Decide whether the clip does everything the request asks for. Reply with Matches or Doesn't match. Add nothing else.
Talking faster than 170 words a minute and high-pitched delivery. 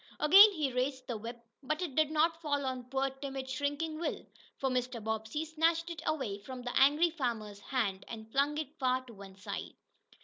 Matches